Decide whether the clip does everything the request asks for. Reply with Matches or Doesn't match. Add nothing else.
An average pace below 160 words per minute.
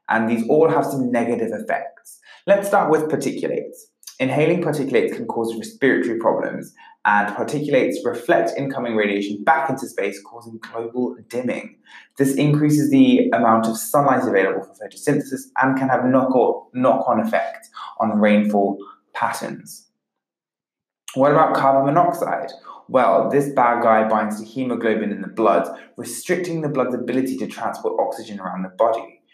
Matches